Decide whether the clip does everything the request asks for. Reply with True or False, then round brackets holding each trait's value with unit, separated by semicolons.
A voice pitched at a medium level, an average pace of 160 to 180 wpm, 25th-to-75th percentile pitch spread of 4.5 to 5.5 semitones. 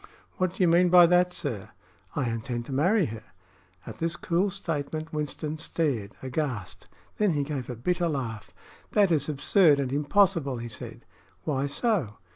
True (150 Hz; 165 wpm; 5.2 semitones)